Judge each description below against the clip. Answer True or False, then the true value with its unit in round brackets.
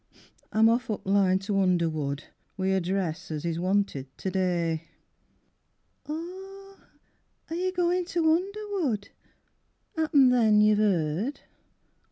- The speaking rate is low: True (125 wpm)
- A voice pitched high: True (205 Hz)